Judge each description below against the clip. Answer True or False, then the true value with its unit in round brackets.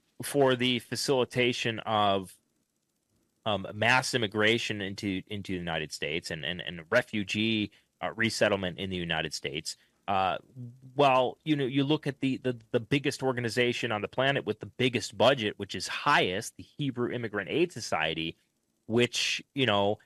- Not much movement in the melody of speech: False (4.1 semitones)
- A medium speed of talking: True (155 wpm)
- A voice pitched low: True (115 Hz)